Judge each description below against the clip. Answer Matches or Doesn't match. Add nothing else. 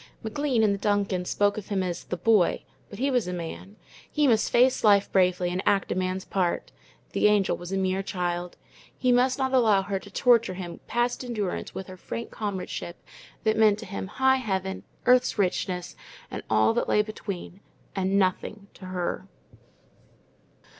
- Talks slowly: Doesn't match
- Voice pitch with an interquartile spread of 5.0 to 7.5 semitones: Doesn't match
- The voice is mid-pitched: Doesn't match